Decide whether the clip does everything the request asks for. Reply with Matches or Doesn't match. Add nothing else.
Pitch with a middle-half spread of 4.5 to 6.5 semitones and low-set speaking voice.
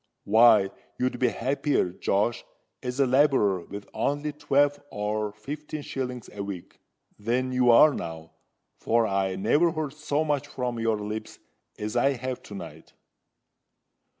Matches